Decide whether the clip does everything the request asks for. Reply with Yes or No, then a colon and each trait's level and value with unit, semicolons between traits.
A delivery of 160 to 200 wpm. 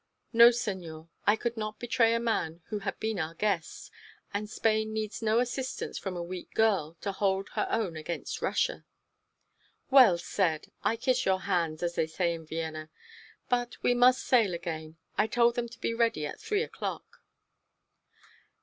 Yes: average, 170 wpm